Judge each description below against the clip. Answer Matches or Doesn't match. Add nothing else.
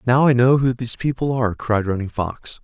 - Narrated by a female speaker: Doesn't match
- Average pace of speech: Doesn't match